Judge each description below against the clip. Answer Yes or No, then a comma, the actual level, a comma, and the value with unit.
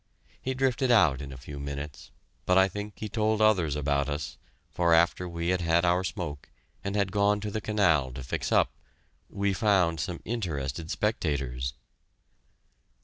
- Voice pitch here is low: Yes, very low, 90 Hz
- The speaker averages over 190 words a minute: No, average, 165 wpm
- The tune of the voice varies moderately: No, wide, 6.1 semitones